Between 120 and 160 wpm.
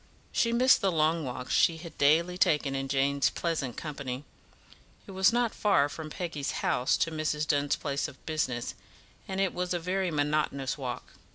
No: average, 175 wpm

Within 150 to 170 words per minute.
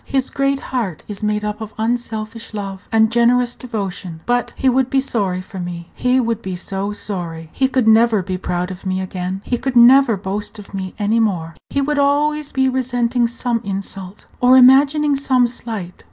No: average, 190 wpm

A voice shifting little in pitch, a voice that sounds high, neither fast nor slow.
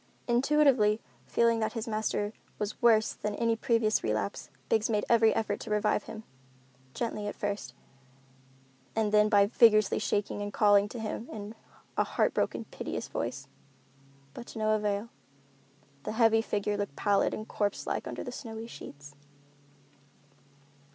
Yes: narrow, 1.6 semitones; high, 215 Hz; average, 150 wpm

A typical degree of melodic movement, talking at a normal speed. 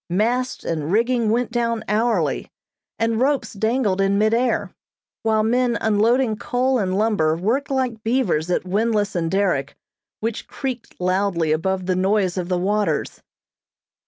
Yes: average, 4.1 semitones; average, 145 wpm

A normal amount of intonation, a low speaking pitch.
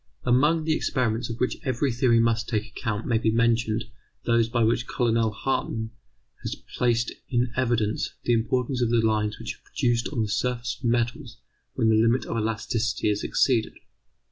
No: narrow, 1.7 semitones; low, 115 Hz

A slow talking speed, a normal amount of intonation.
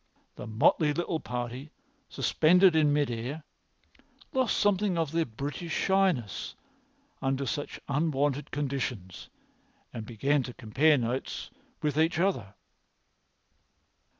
Yes: slow, 110 wpm; average, 4.8 semitones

